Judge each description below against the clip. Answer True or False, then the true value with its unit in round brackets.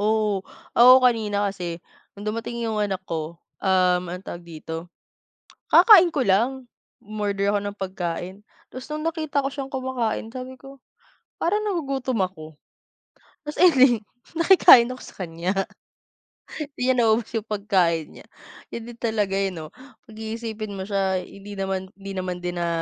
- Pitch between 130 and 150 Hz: False (210 Hz)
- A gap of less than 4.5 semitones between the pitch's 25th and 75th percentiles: False (4.9 semitones)